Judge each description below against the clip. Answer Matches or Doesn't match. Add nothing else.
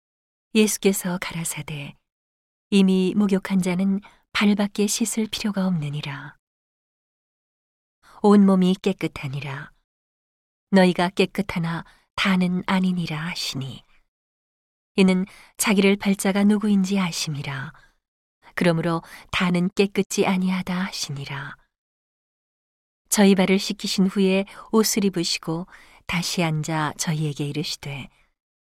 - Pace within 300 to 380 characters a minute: Doesn't match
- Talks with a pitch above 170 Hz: Matches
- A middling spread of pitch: Matches